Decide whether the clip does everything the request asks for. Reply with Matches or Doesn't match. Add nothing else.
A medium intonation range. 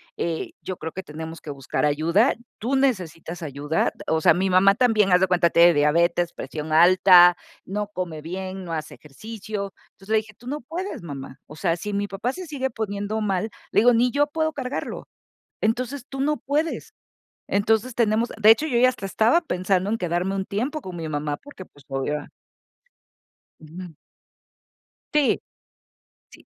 Doesn't match